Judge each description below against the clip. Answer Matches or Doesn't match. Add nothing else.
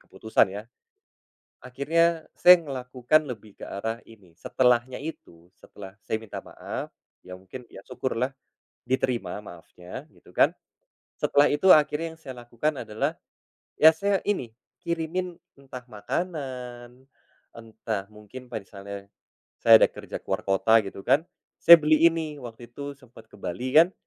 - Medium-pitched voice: Doesn't match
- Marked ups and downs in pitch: Matches